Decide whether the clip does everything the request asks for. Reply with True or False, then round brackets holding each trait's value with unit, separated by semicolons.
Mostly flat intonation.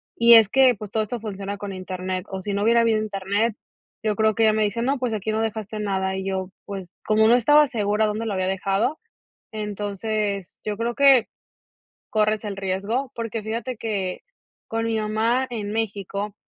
True (2.3 semitones)